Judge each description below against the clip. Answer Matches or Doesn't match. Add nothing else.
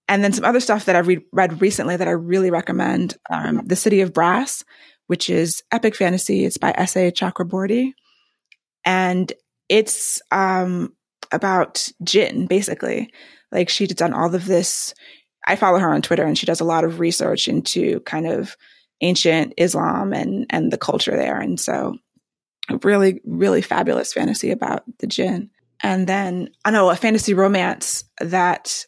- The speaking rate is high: Doesn't match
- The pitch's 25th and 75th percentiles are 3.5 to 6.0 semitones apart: Doesn't match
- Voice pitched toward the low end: Doesn't match